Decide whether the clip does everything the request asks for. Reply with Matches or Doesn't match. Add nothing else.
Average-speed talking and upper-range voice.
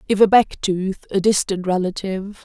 Matches